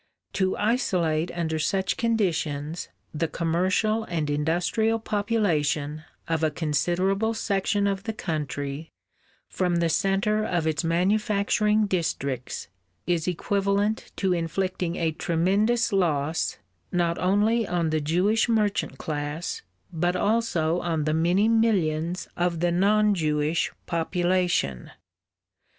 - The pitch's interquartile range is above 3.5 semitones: Yes, average, 4.2 semitones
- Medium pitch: Yes, medium, 175 Hz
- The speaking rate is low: Yes, slow, 115 wpm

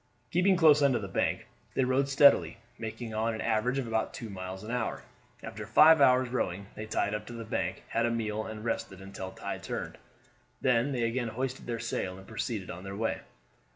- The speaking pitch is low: Yes, low, 115 Hz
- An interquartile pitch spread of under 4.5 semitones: Yes, average, 3.1 semitones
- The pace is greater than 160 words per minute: Yes, average, 200 wpm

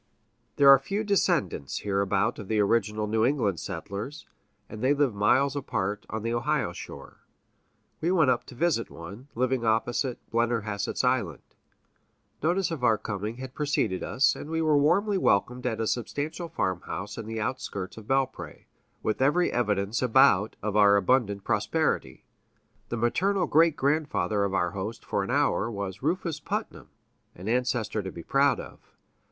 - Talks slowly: No, average, 160 wpm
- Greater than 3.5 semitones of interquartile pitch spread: Yes, wide, 5.5 semitones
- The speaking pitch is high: No, low, 115 Hz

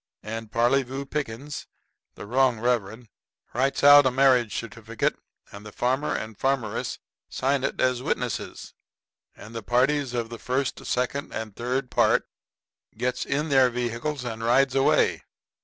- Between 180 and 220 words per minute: No, average, 140 wpm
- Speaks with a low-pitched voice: Yes, low, 125 Hz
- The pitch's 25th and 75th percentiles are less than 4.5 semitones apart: Yes, average, 2.9 semitones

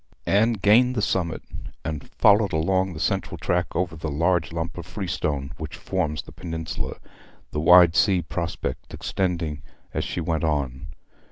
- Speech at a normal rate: Yes, average, 155 wpm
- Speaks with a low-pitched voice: Yes, very low, 85 Hz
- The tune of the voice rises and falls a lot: No, average, 3.1 semitones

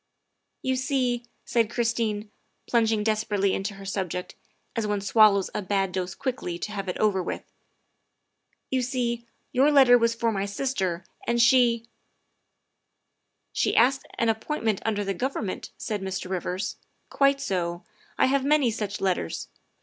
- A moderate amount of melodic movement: Yes, average, 4.0 semitones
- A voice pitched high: Yes, high, 220 Hz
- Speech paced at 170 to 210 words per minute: No, average, 160 wpm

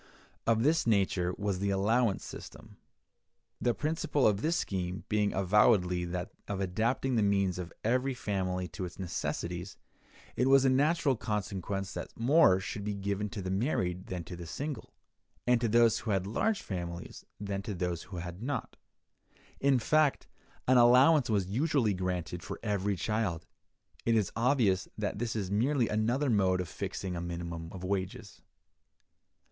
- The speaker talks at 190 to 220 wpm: No, average, 165 wpm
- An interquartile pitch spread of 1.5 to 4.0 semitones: No, average, 4.7 semitones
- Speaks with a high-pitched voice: No, low, 100 Hz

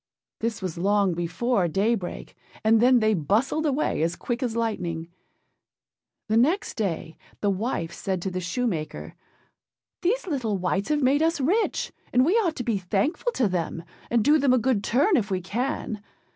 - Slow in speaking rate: No, average, 170 wpm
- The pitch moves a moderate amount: No, wide, 6.1 semitones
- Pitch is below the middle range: No, high, 225 Hz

